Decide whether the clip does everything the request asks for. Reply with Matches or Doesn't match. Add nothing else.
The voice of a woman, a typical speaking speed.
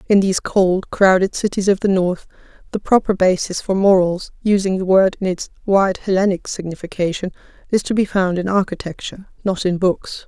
Matches